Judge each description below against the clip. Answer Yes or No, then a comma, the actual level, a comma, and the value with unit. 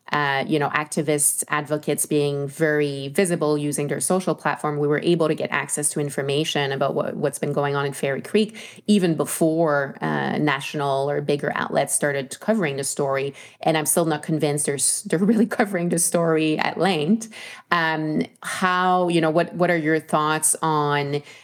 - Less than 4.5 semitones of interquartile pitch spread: Yes, average, 2.9 semitones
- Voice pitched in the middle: Yes, medium, 150 Hz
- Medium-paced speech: Yes, average, 180 wpm